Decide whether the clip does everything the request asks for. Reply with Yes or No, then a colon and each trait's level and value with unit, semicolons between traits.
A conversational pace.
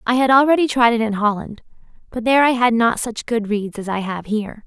No: fast, 245 wpm